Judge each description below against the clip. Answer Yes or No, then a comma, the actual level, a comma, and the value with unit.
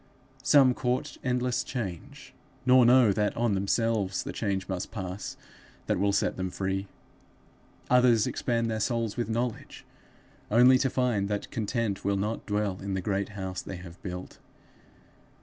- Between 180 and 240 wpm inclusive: No, average, 150 wpm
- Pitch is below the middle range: Yes, low, 105 Hz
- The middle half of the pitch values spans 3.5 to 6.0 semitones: Yes, average, 4.0 semitones